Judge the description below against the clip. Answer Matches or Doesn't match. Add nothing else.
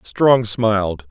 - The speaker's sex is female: Doesn't match